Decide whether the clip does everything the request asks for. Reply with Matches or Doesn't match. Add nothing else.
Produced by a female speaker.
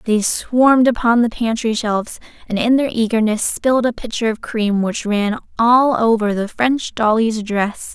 Matches